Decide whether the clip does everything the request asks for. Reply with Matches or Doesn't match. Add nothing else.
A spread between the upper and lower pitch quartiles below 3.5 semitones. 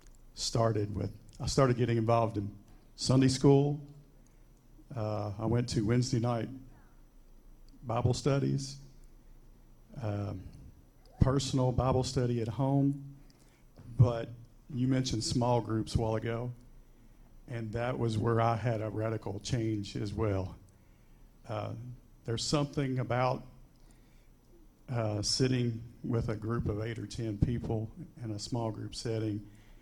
Matches